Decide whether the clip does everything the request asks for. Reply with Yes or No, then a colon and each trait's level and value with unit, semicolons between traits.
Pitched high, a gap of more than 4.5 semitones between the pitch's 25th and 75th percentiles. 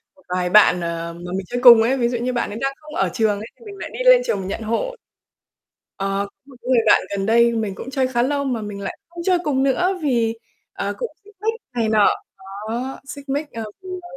Yes: high, 240 Hz; average, 5.1 semitones